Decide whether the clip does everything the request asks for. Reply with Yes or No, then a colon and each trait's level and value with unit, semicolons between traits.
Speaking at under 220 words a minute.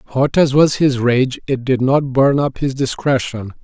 Yes: average, 200 wpm